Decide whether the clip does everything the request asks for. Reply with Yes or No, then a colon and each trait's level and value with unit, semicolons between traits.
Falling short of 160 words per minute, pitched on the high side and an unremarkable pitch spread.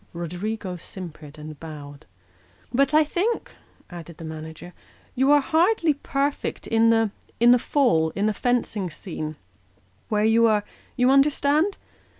No: average, 140 wpm; high, 220 Hz; wide, 9.0 semitones